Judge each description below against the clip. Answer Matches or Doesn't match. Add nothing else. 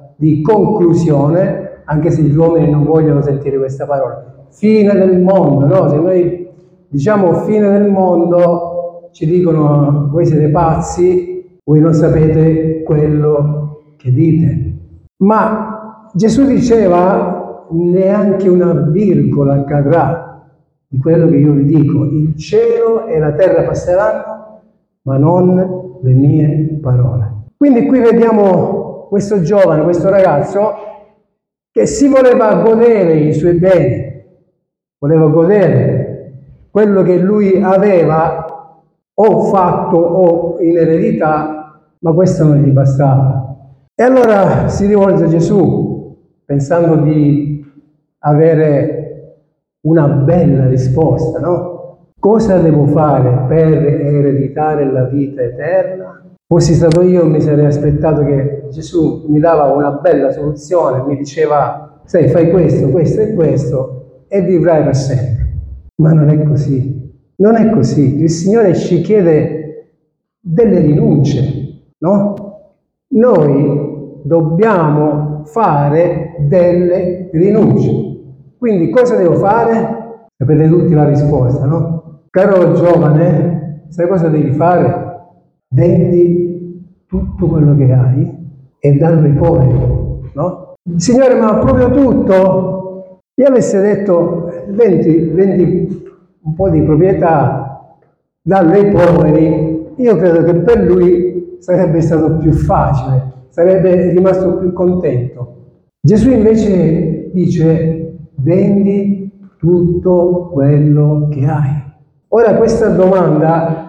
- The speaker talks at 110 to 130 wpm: Matches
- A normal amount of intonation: Matches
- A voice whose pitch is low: Doesn't match